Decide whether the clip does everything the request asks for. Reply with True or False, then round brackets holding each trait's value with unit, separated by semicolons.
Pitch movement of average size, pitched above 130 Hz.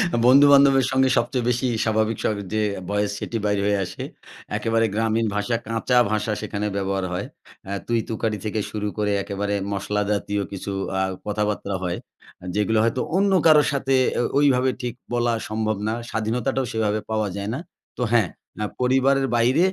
False (3.2 semitones; 110 Hz)